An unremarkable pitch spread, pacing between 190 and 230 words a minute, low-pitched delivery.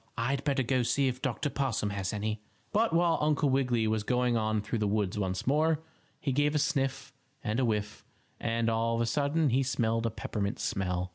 Yes: average, 4.3 semitones; fast, 205 wpm; low, 120 Hz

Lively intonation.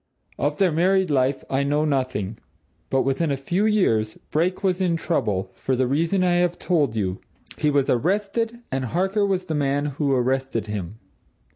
Yes: wide, 5.7 semitones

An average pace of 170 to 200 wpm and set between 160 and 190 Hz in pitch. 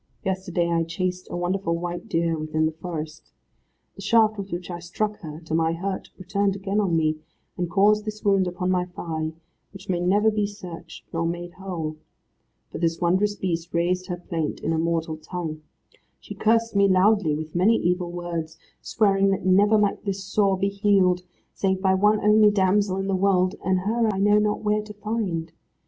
Yes: average, 190 wpm; medium, 185 Hz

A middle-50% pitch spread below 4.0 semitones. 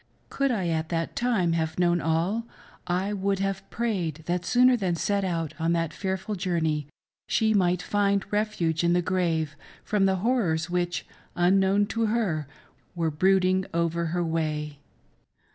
Yes: average, 3.3 semitones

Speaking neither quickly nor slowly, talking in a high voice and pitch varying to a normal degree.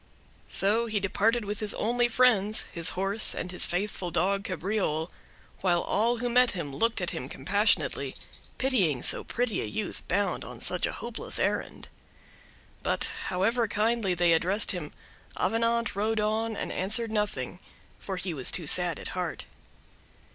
Yes: average, 155 wpm; high, 205 Hz; average, 4.0 semitones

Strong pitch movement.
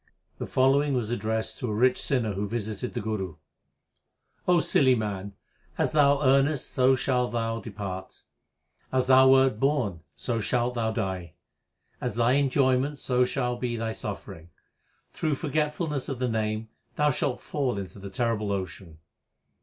No: average, 4.0 semitones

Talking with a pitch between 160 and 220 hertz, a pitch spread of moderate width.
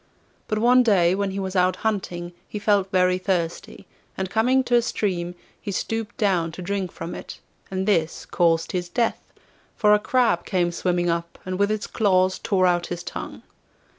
Yes: high, 190 Hz; average, 3.0 semitones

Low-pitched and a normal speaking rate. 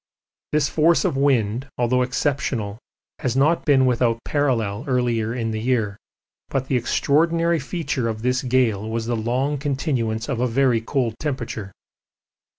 Yes: low, 125 Hz; average, 150 wpm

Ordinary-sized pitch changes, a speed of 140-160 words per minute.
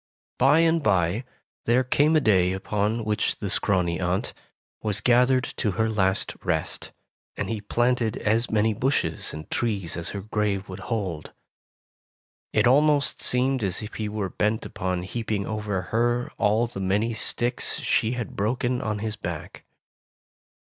Yes: average, 3.7 semitones; average, 155 wpm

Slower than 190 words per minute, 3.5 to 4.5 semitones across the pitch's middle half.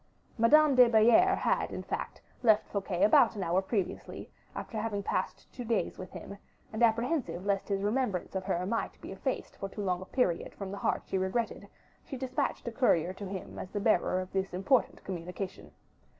No: average, 195 wpm; average, 3.8 semitones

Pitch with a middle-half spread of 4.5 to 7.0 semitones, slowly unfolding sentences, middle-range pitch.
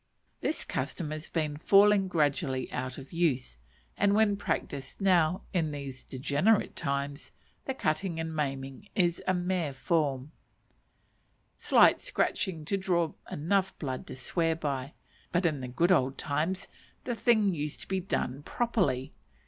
No: average, 5.3 semitones; average, 145 wpm; medium, 160 Hz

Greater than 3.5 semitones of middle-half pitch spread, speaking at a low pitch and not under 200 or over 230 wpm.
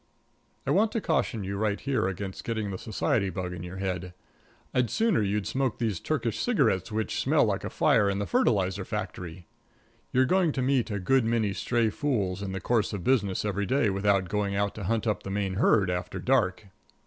Yes: average, 3.9 semitones; low, 105 Hz; fast, 205 wpm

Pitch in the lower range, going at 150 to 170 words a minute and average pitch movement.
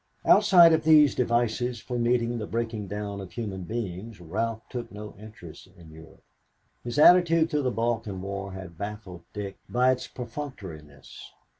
Yes: low, 115 Hz; average, 155 wpm; average, 4.1 semitones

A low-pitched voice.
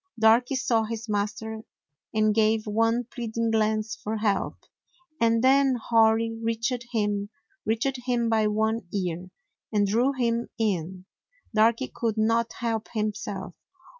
No: high, 225 Hz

